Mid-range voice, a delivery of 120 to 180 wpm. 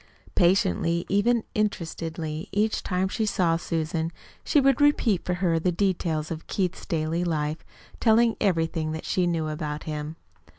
Yes: medium, 170 Hz; average, 145 wpm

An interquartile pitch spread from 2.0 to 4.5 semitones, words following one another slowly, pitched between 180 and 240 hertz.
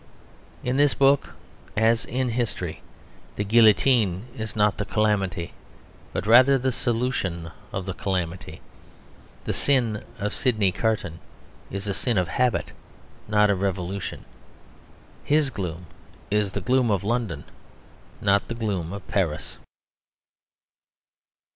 No: average, 4.1 semitones; slow, 120 wpm; low, 105 Hz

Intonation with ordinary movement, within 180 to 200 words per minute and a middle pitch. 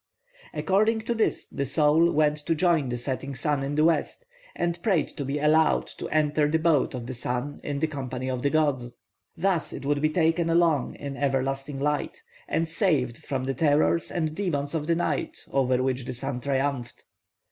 Yes: average, 3.3 semitones; average, 190 wpm; medium, 145 Hz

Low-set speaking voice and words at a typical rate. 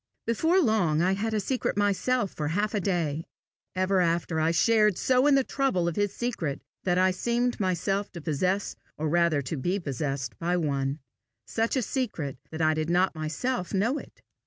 No: medium, 185 Hz; average, 185 wpm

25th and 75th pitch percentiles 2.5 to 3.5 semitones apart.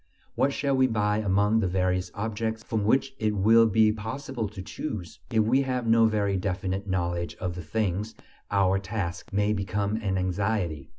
Yes: average, 2.9 semitones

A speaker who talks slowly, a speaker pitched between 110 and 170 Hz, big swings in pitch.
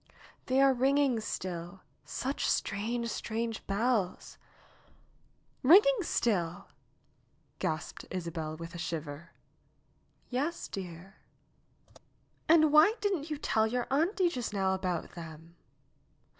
No: slow, 110 wpm; high, 220 Hz; wide, 8.1 semitones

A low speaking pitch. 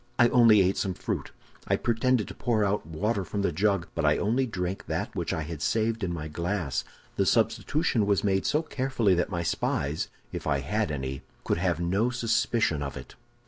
Yes: low, 100 Hz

